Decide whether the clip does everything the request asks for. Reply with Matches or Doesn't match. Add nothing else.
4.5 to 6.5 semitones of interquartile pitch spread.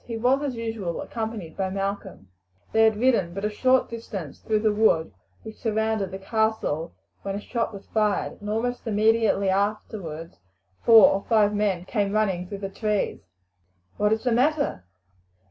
Doesn't match